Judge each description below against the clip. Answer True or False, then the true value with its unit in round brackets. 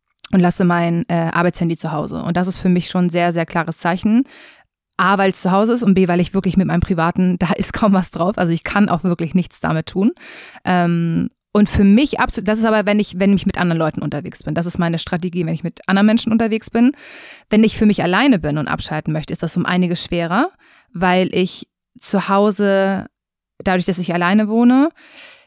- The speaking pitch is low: False (185 Hz)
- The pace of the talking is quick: True (225 wpm)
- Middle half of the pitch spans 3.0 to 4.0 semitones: True (3.6 semitones)